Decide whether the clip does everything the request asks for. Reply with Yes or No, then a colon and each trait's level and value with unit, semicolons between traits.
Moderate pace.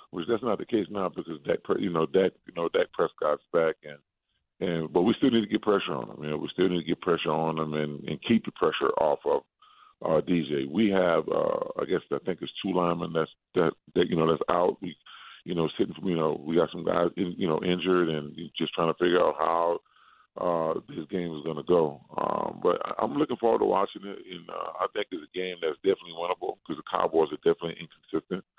No: fast, 245 wpm